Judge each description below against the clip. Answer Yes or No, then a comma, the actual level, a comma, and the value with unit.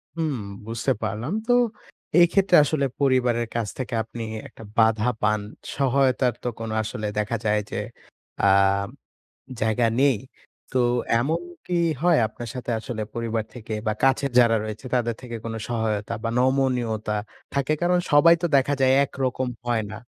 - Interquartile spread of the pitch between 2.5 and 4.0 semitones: Yes, average, 3.4 semitones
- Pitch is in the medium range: No, low, 120 Hz